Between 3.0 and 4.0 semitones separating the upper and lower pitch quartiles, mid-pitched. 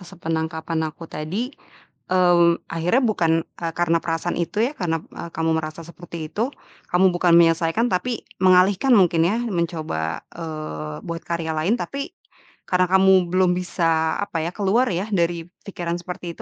No: narrow, 2.5 semitones; medium, 175 Hz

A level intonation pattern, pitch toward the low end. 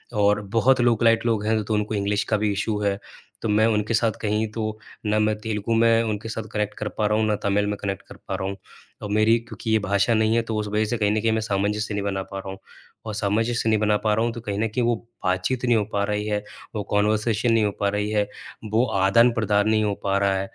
Yes: narrow, 1.6 semitones; low, 105 Hz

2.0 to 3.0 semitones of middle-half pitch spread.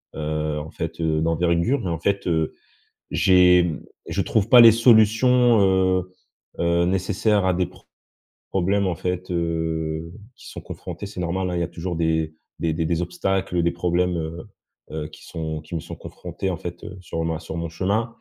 Yes: narrow, 2.5 semitones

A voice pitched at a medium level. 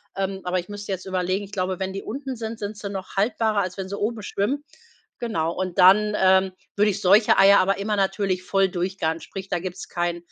No: high, 195 Hz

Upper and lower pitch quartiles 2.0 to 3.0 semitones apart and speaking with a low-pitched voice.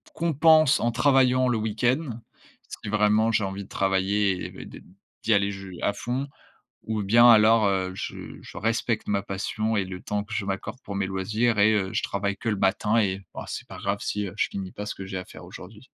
Yes: average, 2.7 semitones; low, 105 Hz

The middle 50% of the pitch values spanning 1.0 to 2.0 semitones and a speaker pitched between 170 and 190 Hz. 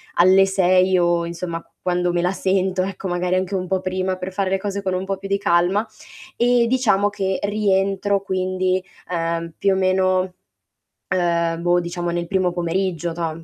Yes: narrow, 1.7 semitones; medium, 185 Hz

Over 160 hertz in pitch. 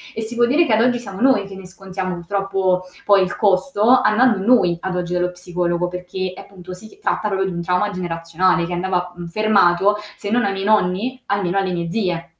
Yes: high, 190 Hz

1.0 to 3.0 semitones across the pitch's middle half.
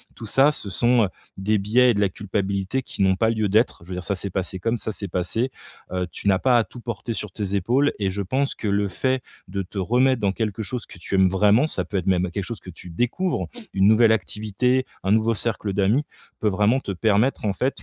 No: average, 3.6 semitones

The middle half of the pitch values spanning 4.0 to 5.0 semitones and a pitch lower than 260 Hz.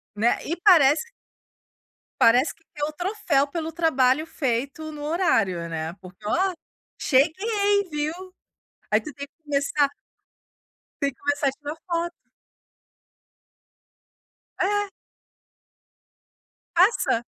No: average, 4.5 semitones; very high, 295 Hz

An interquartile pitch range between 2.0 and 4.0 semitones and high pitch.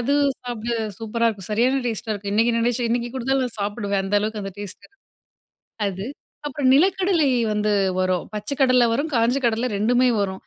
Yes: average, 3.4 semitones; high, 230 Hz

